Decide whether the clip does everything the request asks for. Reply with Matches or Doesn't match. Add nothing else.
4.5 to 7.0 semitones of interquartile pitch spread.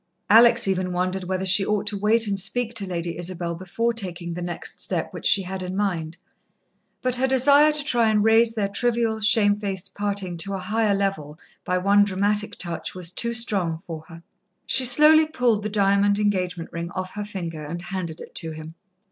Doesn't match